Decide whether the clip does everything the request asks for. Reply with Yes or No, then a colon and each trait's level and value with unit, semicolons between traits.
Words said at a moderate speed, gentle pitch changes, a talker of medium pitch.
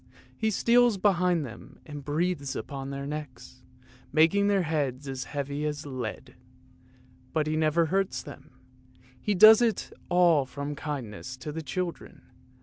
No: average, 145 wpm; average, 4.4 semitones; medium, 150 Hz